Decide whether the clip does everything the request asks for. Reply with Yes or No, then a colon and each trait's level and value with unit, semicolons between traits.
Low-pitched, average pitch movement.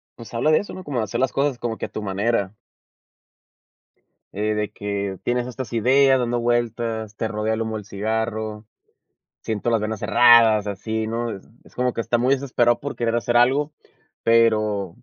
No: low, 115 Hz; narrow, 2.1 semitones